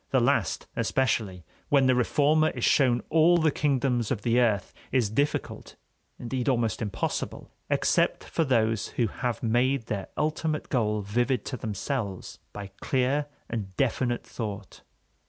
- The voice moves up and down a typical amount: Yes, average, 4.1 semitones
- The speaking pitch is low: Yes, low, 120 Hz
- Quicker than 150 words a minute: No, average, 140 wpm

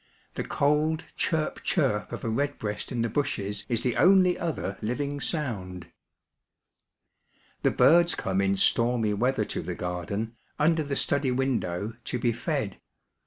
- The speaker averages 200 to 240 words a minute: No, average, 145 wpm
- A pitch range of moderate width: No, wide, 5.9 semitones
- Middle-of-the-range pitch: No, low, 125 Hz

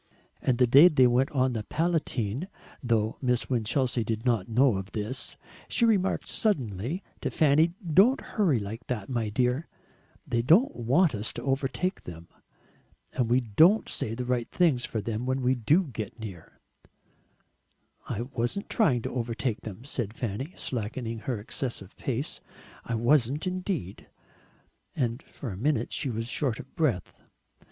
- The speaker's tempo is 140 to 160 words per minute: Yes, average, 155 wpm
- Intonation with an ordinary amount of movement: Yes, average, 4.2 semitones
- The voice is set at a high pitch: No, low, 125 Hz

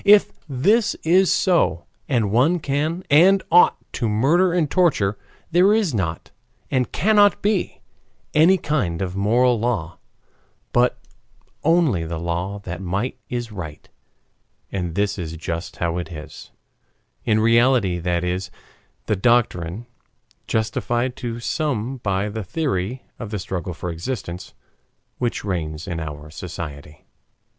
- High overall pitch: No, low, 110 Hz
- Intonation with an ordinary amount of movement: No, wide, 8.3 semitones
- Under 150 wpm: Yes, slow, 135 wpm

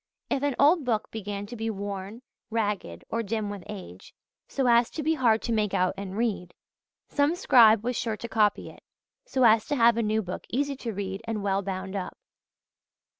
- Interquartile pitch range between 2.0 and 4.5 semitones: Yes, average, 3.2 semitones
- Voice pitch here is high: Yes, high, 220 Hz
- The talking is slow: No, average, 200 wpm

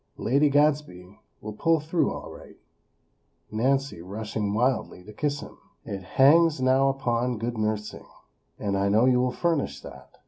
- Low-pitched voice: Yes, low, 125 Hz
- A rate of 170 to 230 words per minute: No, average, 150 wpm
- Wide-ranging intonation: No, average, 5.0 semitones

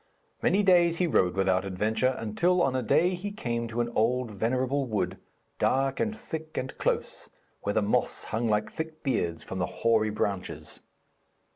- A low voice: Yes, low, 120 Hz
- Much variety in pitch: Yes, wide, 6.9 semitones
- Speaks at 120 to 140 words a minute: No, average, 175 wpm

